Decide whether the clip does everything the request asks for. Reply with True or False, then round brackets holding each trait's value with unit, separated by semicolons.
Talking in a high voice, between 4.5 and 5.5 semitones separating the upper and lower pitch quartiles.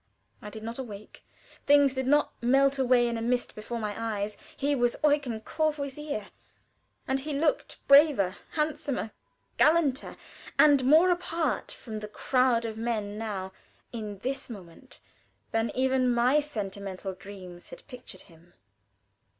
True (245 Hz; 4.8 semitones)